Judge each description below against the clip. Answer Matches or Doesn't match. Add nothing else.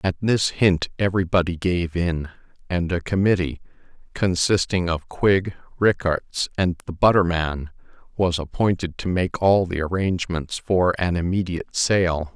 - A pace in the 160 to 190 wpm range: Doesn't match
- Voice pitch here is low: Matches